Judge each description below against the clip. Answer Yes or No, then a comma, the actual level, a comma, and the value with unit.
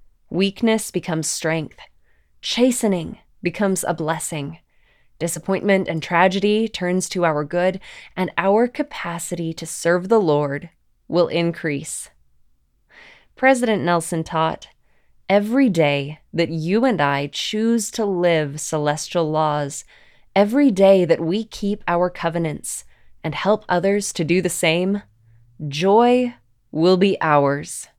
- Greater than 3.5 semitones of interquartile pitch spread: Yes, average, 4.1 semitones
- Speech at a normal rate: No, slow, 120 wpm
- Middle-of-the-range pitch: Yes, medium, 175 Hz